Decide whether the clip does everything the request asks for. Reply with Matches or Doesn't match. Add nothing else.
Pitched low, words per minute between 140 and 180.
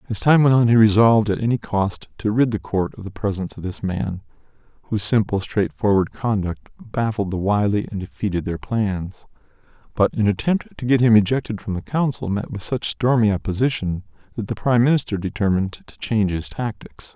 Doesn't match